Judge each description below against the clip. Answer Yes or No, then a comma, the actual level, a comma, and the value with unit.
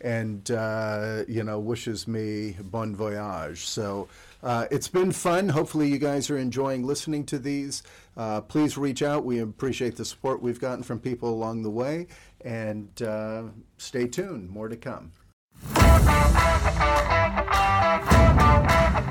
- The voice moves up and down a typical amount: Yes, average, 4.4 semitones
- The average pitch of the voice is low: Yes, low, 115 Hz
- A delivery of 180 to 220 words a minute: No, slow, 135 wpm